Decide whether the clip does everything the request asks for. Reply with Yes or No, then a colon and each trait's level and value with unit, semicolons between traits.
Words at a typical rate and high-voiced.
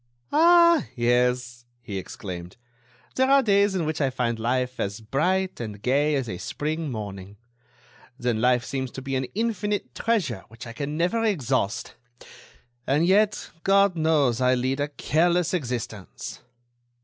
No: average, 150 wpm; low, 135 Hz